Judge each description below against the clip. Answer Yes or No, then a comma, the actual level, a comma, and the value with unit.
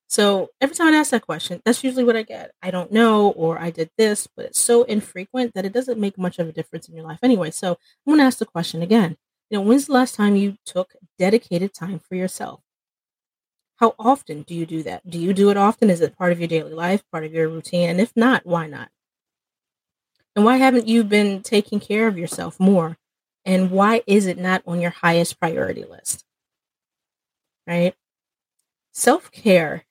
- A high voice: Yes, high, 195 Hz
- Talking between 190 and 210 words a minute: Yes, fast, 205 wpm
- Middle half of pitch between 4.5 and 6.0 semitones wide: Yes, average, 4.9 semitones